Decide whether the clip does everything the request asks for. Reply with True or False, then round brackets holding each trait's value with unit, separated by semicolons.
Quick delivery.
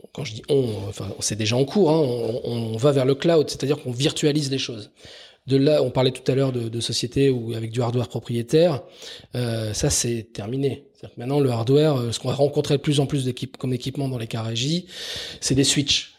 True (225 wpm)